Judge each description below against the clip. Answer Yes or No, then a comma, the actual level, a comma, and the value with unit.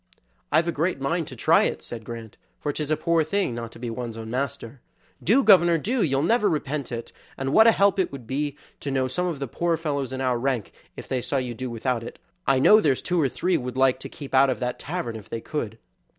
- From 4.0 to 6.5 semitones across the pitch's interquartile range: Yes, average, 5.2 semitones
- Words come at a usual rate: No, fast, 250 wpm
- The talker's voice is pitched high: No, low, 135 Hz